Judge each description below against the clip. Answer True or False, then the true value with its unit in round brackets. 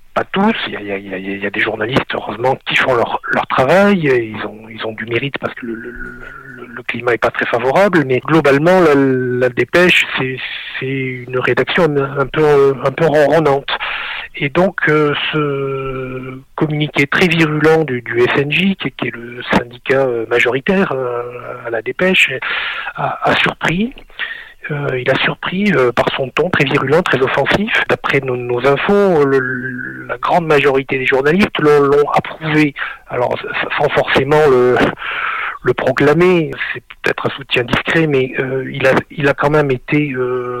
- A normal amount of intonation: True (3.4 semitones)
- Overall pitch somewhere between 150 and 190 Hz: False (135 Hz)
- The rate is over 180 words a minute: False (175 wpm)